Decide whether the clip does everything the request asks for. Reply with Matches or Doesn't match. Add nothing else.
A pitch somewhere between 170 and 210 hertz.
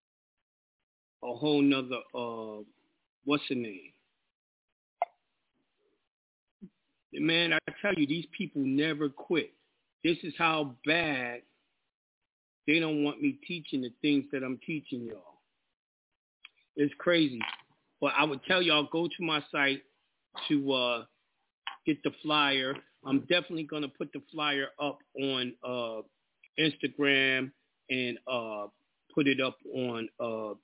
Doesn't match